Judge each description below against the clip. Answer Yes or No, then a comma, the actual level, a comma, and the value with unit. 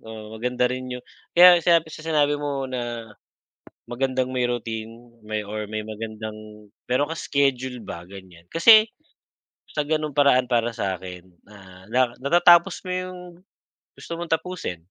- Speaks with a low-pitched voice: Yes, low, 125 Hz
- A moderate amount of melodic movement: No, wide, 5.8 semitones